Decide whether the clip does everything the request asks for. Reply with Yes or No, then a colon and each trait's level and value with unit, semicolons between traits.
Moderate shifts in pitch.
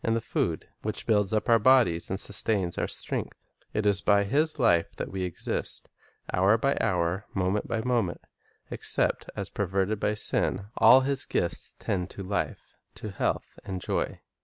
Yes: average, 3.2 semitones